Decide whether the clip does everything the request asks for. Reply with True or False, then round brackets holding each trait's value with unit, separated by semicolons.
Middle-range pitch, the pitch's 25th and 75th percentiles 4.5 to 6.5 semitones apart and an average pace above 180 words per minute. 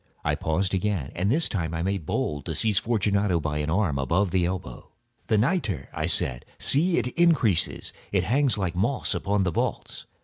False (95 Hz; 5.0 semitones; 190 wpm)